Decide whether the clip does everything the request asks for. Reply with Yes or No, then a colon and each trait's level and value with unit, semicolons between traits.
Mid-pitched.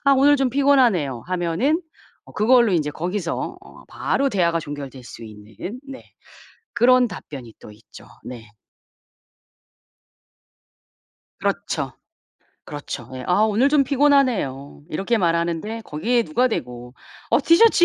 No: high, 195 Hz